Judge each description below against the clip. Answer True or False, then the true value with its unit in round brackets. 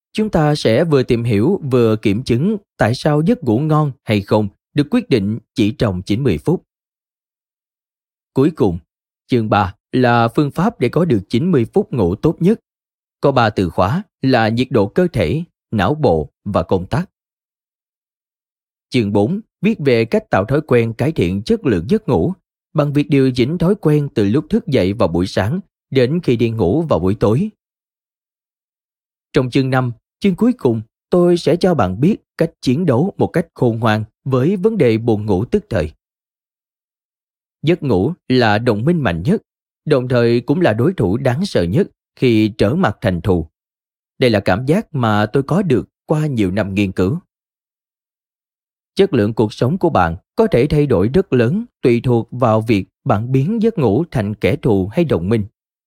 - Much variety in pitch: True (7.2 semitones)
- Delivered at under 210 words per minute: True (185 wpm)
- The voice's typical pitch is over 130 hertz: False (125 Hz)